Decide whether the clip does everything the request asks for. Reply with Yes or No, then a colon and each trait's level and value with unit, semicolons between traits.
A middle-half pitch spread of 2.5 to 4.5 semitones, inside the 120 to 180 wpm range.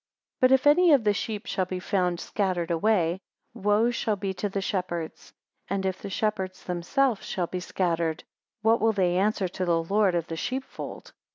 No: average, 3.4 semitones; average, 195 wpm